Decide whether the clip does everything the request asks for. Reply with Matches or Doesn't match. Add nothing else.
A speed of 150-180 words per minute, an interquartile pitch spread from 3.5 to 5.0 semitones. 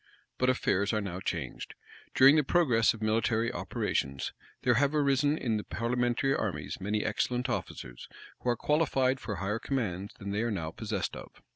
Matches